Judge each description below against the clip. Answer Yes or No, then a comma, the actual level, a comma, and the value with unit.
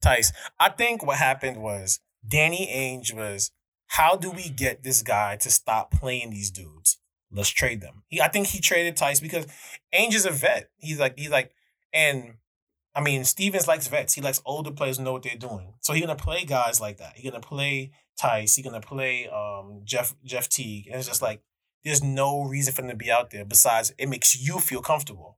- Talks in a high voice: No, low, 130 Hz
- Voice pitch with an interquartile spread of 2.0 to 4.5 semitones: No, average, 4.9 semitones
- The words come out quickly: Yes, fast, 210 wpm